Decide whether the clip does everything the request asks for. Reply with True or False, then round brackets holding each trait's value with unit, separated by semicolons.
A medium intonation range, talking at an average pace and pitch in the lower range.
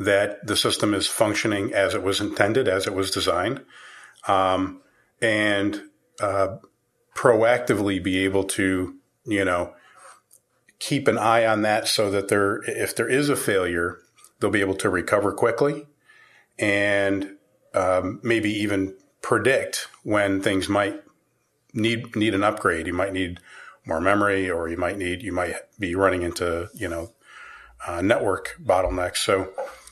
False (1.7 semitones; 145 wpm; 100 Hz)